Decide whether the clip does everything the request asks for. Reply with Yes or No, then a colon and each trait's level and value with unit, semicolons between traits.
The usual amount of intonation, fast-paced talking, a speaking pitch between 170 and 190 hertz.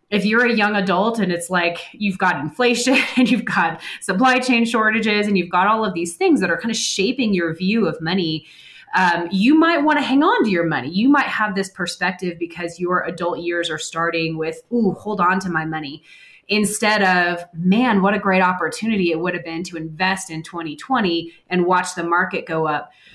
Yes: average, 4.1 semitones; fast, 215 wpm; medium, 185 Hz